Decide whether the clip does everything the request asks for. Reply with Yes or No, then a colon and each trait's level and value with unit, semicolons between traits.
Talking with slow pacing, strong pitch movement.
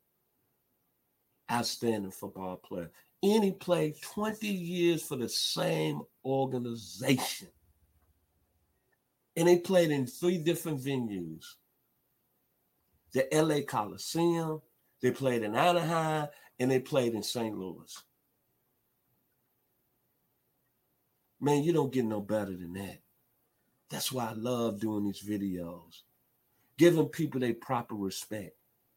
Yes: slow, 110 wpm; wide, 7.4 semitones